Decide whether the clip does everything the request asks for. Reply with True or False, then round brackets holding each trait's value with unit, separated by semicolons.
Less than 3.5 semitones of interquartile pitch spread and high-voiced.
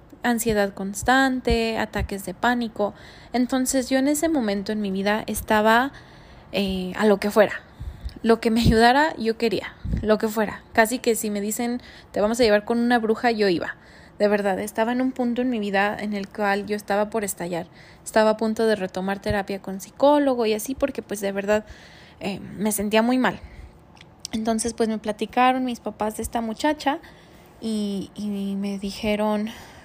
True (2.8 semitones; 215 Hz)